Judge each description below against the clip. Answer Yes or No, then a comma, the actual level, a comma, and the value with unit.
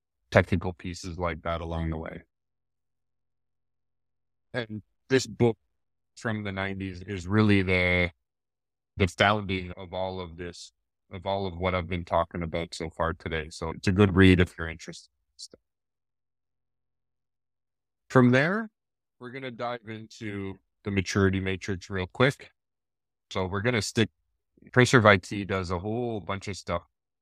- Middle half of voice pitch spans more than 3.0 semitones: Yes, average, 3.5 semitones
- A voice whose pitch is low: Yes, very low, 95 Hz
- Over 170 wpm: No, average, 150 wpm